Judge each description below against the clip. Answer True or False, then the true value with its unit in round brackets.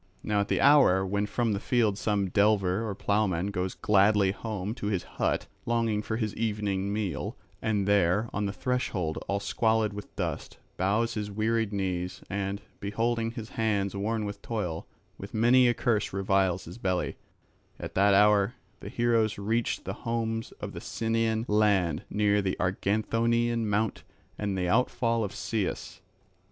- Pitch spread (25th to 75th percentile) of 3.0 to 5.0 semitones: False (2.4 semitones)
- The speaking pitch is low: True (105 Hz)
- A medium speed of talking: True (160 wpm)